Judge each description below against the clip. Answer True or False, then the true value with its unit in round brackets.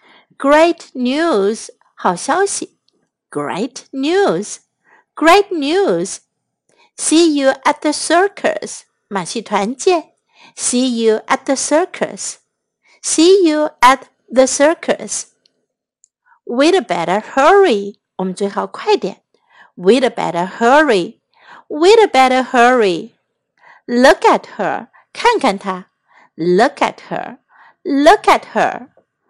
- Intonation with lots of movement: True (6.5 semitones)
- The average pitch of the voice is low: False (295 Hz)